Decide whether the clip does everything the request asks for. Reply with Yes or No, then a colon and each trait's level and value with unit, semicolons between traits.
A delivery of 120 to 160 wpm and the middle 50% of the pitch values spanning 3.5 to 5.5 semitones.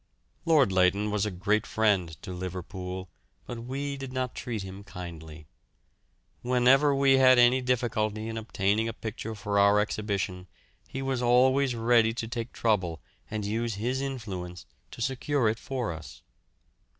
Yes: average, 150 wpm; average, 4.5 semitones